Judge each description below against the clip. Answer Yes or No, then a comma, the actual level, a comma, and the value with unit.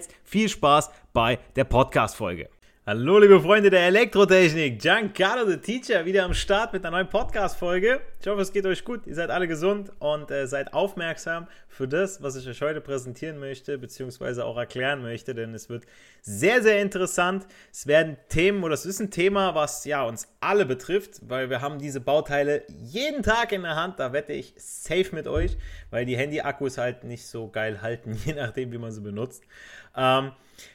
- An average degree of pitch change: No, wide, 6.8 semitones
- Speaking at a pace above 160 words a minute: Yes, fast, 190 wpm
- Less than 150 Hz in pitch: No, medium, 155 Hz